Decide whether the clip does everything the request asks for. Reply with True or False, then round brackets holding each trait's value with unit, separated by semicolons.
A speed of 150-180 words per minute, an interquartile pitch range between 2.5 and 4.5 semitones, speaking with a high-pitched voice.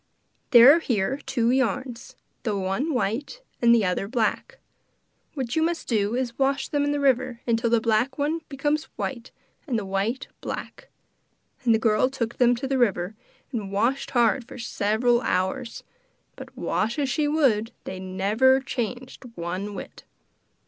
True (165 wpm; 3.8 semitones; 240 Hz)